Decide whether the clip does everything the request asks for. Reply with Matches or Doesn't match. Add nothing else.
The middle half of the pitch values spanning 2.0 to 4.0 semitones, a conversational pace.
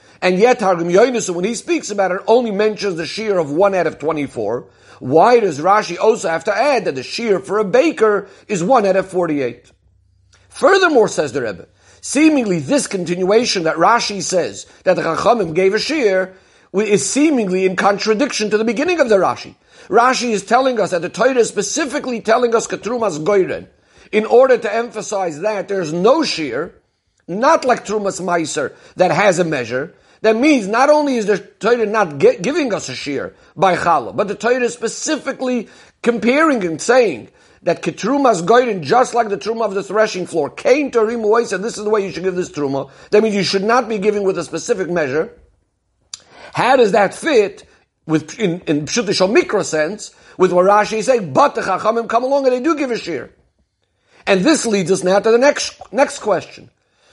Doesn't match